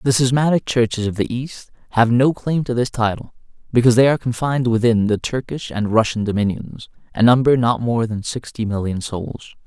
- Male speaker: Yes, male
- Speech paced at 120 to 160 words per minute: No, average, 185 wpm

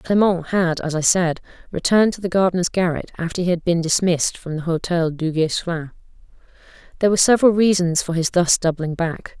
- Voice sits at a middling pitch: Yes, medium, 175 Hz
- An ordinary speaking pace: Yes, average, 180 wpm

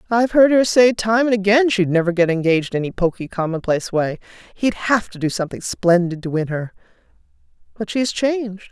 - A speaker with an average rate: Yes, average, 195 wpm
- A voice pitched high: Yes, high, 200 Hz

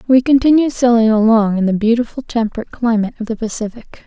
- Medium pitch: No, high, 230 Hz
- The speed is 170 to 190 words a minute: Yes, average, 175 wpm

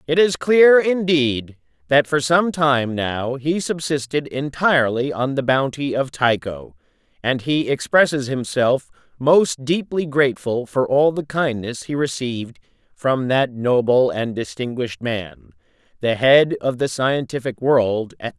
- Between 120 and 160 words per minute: Yes, average, 145 wpm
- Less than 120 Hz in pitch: No, low, 135 Hz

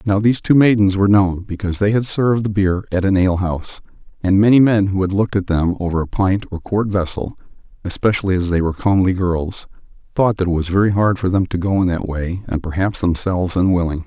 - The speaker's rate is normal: No, fast, 225 wpm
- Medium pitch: No, very low, 95 Hz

